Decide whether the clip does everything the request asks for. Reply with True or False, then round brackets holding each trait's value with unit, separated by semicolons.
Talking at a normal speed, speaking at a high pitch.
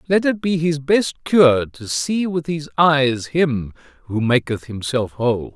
False (175 wpm; 140 Hz)